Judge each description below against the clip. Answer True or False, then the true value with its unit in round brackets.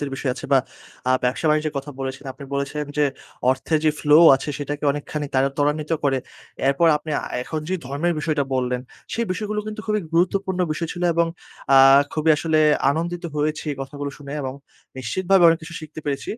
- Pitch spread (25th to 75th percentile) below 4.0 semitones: True (3.2 semitones)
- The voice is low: False (150 Hz)